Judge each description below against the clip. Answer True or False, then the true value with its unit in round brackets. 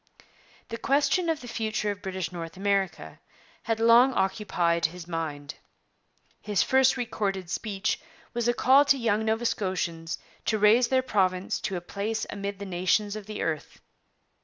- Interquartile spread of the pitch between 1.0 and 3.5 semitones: False (4.2 semitones)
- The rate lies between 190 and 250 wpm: False (160 wpm)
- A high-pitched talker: True (205 Hz)